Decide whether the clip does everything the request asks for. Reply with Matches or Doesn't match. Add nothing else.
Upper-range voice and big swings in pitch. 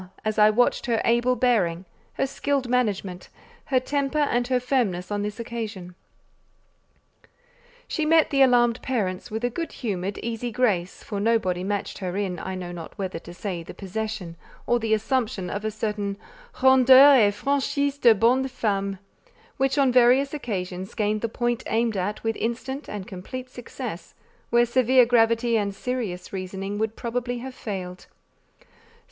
Doesn't match